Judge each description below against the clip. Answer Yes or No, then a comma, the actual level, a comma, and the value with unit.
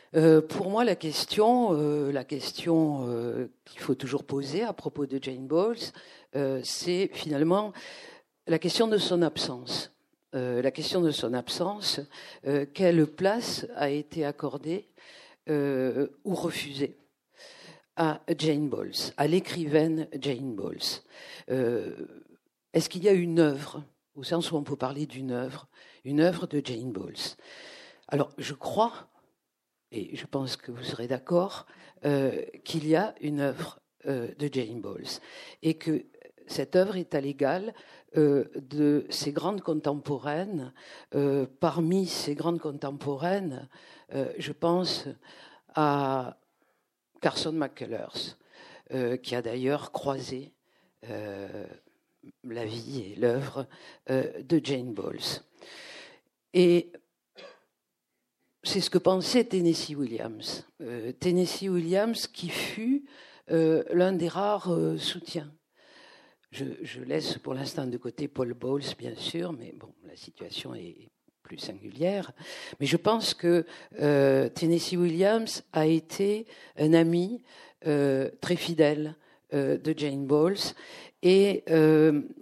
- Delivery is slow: Yes, slow, 125 wpm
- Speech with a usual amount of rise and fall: Yes, average, 4.1 semitones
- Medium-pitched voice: Yes, medium, 155 Hz